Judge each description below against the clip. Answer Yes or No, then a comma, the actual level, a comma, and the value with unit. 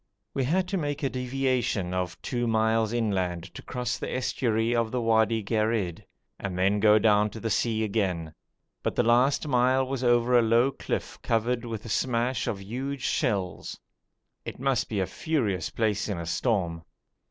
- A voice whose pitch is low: Yes, low, 115 Hz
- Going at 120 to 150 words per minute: No, average, 175 wpm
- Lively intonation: No, average, 3.5 semitones